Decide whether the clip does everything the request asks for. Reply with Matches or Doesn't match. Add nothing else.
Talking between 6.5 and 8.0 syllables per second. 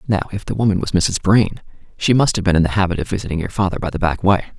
Matches